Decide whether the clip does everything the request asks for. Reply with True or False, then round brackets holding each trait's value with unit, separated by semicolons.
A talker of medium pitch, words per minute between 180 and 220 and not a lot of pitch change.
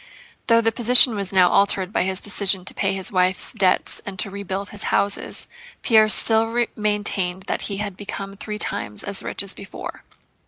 False (200 Hz; 185 wpm; 1.9 semitones)